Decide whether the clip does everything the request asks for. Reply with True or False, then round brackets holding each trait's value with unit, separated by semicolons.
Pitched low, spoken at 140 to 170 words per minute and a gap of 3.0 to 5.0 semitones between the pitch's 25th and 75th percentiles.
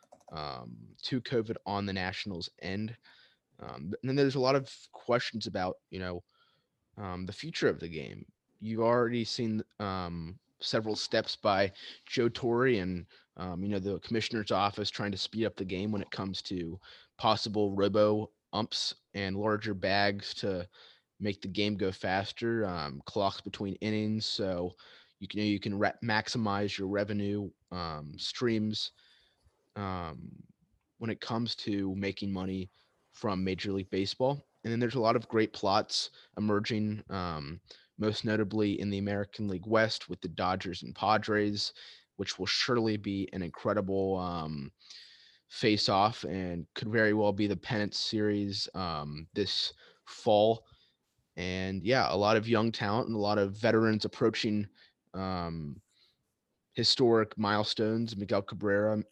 False (105 Hz; 150 wpm; 2.5 semitones)